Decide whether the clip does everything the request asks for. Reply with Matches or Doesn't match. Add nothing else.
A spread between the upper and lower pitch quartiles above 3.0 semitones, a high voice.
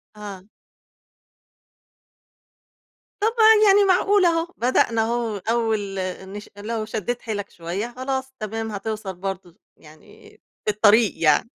Matches